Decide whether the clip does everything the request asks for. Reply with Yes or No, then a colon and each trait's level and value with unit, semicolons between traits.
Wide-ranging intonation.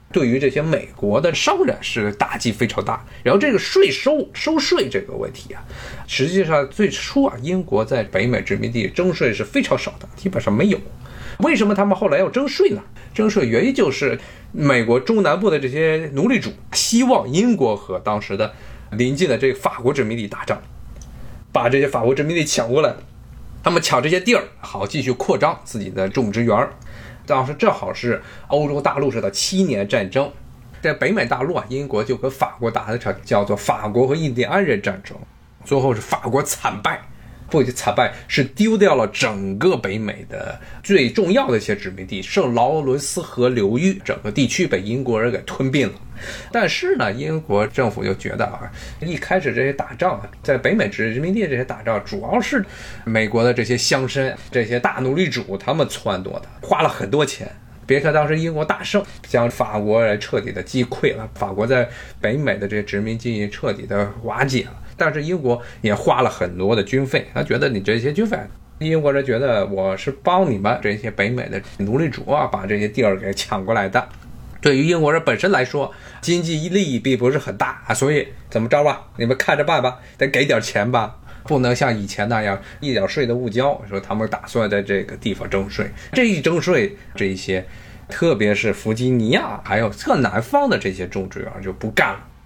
Yes: wide, 6.8 semitones